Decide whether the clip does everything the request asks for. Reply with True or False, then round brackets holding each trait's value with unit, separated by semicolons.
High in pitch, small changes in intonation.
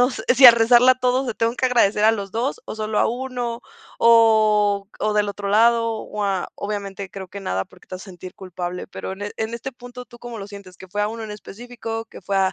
False (215 Hz; 3.0 semitones)